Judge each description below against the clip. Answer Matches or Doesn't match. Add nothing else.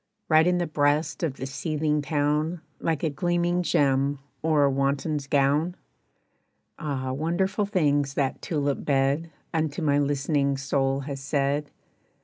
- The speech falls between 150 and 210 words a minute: Doesn't match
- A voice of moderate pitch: Matches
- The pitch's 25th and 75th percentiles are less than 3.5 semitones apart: Matches